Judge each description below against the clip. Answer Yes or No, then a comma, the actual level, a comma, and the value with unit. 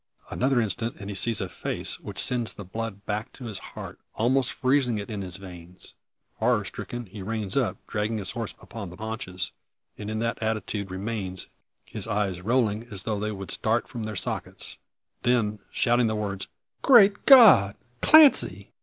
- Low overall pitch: Yes, low, 110 Hz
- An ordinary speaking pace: Yes, average, 175 wpm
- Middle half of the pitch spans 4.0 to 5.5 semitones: No, average, 3.0 semitones